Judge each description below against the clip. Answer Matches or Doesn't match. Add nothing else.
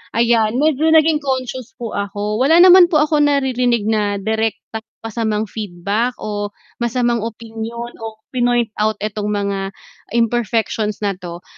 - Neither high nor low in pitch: Doesn't match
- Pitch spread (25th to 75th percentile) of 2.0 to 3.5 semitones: Matches